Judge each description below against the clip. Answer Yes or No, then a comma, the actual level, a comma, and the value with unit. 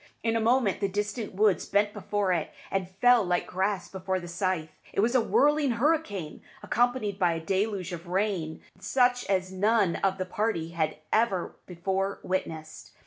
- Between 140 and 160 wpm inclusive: No, average, 170 wpm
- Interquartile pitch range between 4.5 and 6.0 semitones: No, average, 3.5 semitones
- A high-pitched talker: Yes, high, 195 Hz